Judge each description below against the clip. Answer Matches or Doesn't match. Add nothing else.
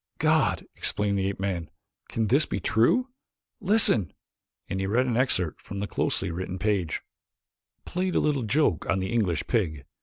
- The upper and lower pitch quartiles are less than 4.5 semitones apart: Doesn't match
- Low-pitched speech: Matches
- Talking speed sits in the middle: Matches